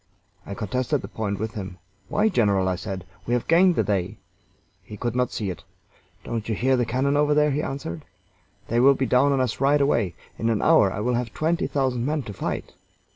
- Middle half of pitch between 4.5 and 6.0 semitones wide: Yes, average, 5.0 semitones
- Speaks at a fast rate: Yes, fast, 220 wpm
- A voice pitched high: No, low, 120 Hz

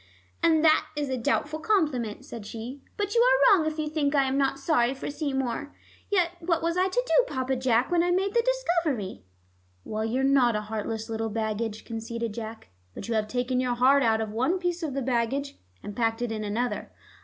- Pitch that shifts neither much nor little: No, wide, 5.9 semitones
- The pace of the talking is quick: Yes, fast, 210 wpm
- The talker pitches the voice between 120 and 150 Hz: No, very high, 265 Hz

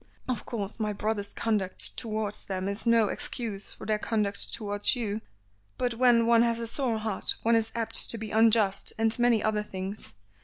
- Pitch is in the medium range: No, high, 220 Hz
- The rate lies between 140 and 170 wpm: No, average, 185 wpm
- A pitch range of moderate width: No, narrow, 2.1 semitones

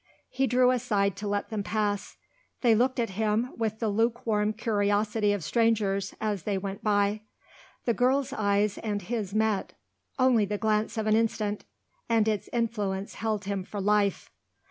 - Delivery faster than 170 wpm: No, average, 165 wpm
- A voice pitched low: No, high, 215 Hz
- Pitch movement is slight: Yes, narrow, 2.0 semitones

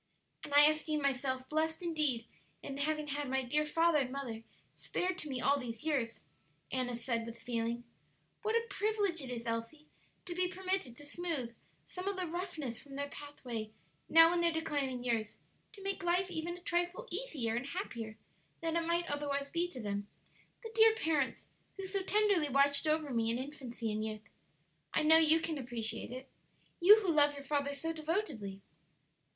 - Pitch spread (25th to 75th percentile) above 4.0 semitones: Yes, wide, 5.5 semitones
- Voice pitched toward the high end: Yes, very high, 290 Hz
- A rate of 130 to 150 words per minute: No, average, 180 wpm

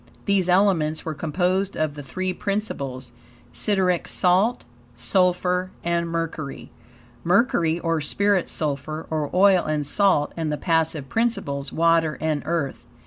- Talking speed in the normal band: No, slow, 130 wpm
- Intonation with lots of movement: No, average, 3.5 semitones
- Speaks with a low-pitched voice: No, medium, 165 Hz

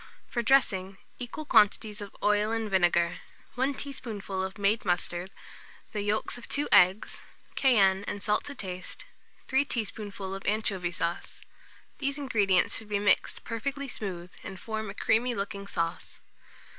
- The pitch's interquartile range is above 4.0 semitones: No, average, 3.4 semitones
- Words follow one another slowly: No, average, 145 wpm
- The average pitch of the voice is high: Yes, high, 205 Hz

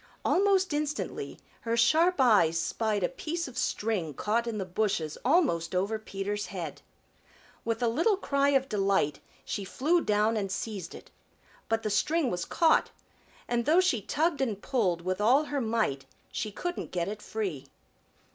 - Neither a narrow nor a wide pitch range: No, wide, 6.3 semitones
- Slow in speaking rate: No, average, 165 wpm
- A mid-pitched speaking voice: No, high, 225 Hz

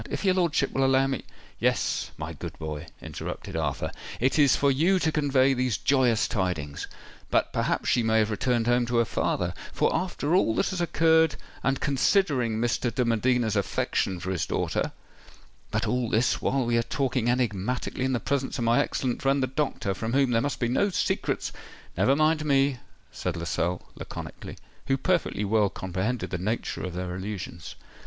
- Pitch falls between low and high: No, low, 125 Hz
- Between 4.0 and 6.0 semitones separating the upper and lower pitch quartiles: Yes, average, 4.5 semitones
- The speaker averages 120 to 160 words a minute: No, average, 175 wpm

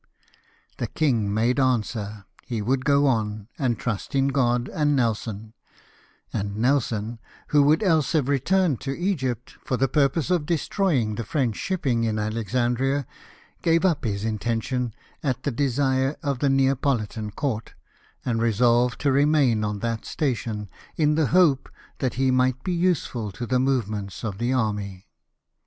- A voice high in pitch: No, low, 125 Hz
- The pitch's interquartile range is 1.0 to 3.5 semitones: No, average, 4.1 semitones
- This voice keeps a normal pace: Yes, average, 150 wpm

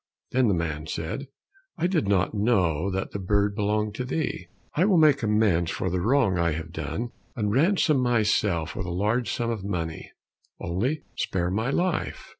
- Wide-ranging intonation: Yes, wide, 5.8 semitones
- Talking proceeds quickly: No, average, 180 wpm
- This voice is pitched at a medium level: No, low, 105 Hz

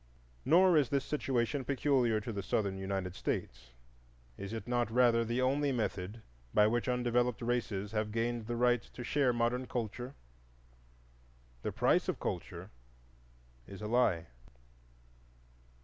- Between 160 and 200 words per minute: No, slow, 135 wpm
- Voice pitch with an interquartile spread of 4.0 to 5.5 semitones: No, average, 2.8 semitones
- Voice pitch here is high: No, low, 120 Hz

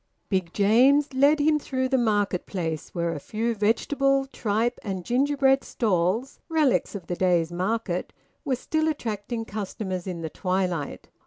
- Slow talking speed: No, average, 150 wpm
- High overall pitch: Yes, high, 220 Hz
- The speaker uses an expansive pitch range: Yes, wide, 6.6 semitones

